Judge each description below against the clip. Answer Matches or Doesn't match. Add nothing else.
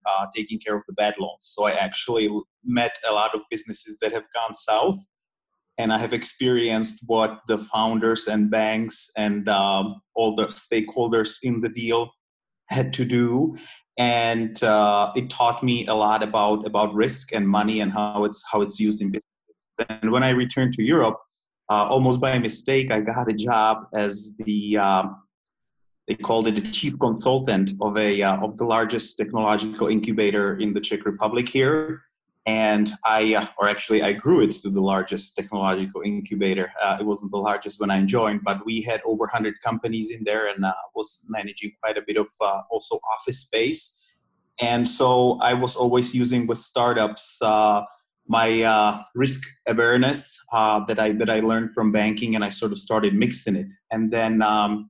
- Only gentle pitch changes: Matches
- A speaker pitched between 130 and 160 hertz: Doesn't match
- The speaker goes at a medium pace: Matches